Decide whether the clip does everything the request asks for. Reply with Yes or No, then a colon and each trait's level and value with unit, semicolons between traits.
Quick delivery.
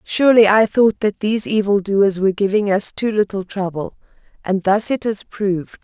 No: average, 185 wpm